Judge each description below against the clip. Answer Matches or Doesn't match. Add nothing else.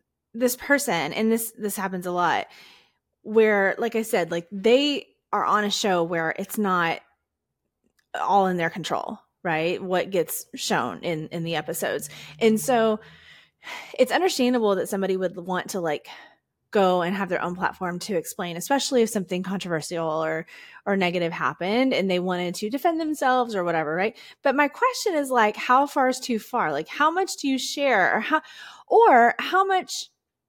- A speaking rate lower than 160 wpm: Doesn't match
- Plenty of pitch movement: Matches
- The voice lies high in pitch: Matches